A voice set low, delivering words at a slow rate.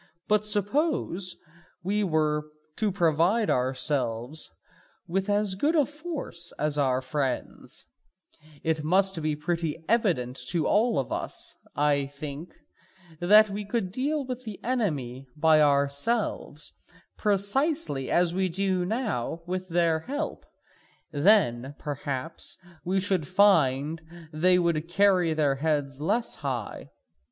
No: medium, 170 Hz; slow, 125 wpm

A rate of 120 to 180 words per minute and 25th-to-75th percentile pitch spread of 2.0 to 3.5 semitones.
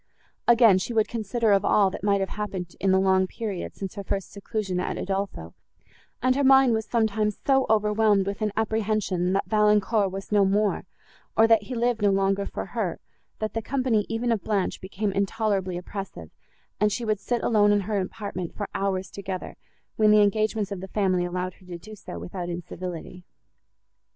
No: average, 190 wpm; narrow, 2.5 semitones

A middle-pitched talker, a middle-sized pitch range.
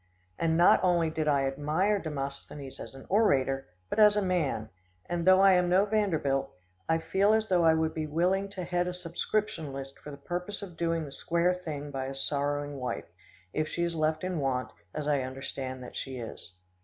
Yes: medium, 160 Hz; average, 4.6 semitones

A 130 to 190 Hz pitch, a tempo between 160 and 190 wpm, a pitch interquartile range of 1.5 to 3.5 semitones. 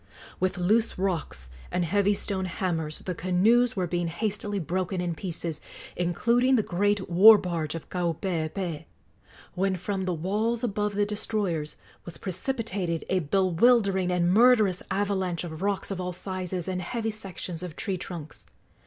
No: medium, 185 Hz; average, 150 wpm; average, 2.9 semitones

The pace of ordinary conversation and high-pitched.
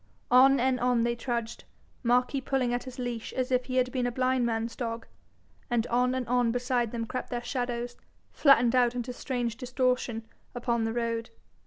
Yes: average, 185 wpm; high, 245 Hz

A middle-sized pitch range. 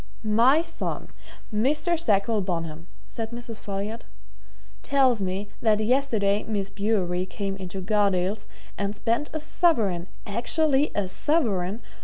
Yes: average, 4.3 semitones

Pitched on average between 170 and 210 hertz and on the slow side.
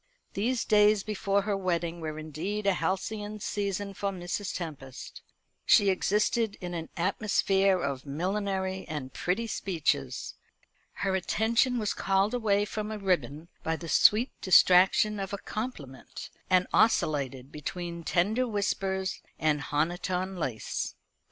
Yes: high, 190 Hz; slow, 130 wpm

